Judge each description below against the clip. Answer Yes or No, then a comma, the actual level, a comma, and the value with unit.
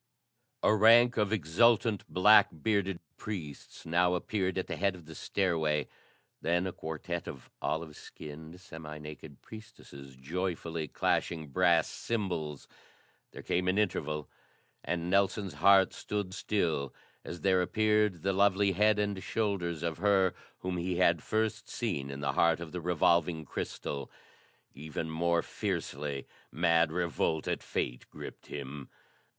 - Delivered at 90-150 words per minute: Yes, average, 140 wpm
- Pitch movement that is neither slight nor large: Yes, average, 4.0 semitones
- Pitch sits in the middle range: No, very low, 85 Hz